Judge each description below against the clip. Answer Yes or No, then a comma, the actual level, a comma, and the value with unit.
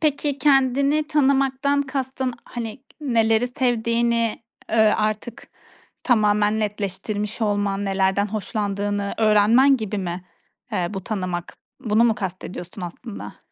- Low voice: No, high, 220 Hz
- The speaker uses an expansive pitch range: No, average, 4.2 semitones